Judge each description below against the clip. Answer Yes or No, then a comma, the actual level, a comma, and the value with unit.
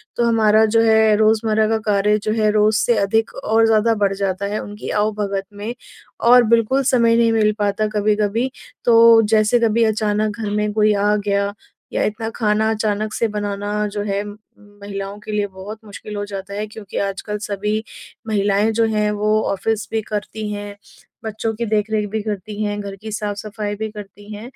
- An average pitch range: No, narrow, 1.2 semitones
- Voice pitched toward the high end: Yes, high, 210 Hz